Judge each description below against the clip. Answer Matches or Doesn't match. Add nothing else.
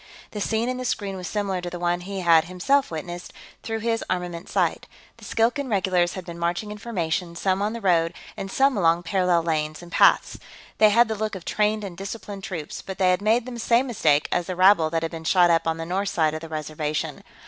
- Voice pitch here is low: Doesn't match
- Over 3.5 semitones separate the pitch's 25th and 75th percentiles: Matches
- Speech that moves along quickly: Matches